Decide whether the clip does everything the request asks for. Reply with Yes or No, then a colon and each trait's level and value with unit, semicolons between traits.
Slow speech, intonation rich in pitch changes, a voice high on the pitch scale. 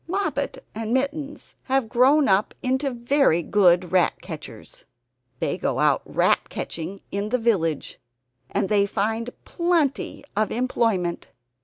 Yes: slow, 130 wpm; wide, 5.9 semitones; high, 225 Hz